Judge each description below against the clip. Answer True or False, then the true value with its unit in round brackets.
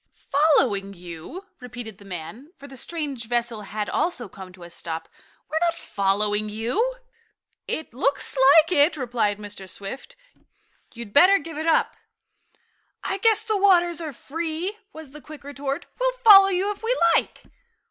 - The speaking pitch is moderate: False (280 Hz)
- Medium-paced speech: True (160 wpm)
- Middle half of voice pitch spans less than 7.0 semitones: False (8.2 semitones)